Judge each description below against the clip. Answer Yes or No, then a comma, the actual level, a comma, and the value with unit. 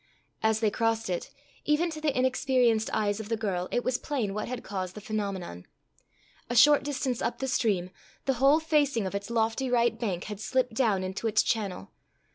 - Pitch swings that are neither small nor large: Yes, average, 4.2 semitones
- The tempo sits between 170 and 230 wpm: Yes, average, 195 wpm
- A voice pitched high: Yes, high, 225 Hz